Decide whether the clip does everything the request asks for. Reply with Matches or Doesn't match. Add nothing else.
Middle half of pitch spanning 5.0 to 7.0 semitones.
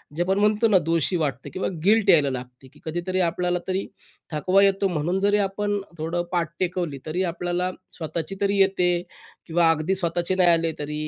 Doesn't match